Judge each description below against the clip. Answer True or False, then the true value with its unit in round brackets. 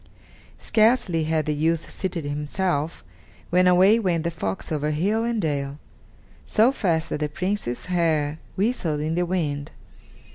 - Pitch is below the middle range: False (165 Hz)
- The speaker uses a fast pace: False (145 wpm)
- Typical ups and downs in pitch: True (3.9 semitones)